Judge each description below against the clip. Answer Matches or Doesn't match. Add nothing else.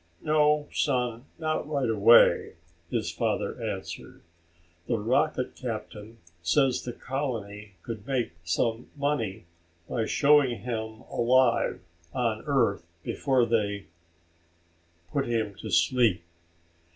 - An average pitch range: Matches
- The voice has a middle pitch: Doesn't match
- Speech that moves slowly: Matches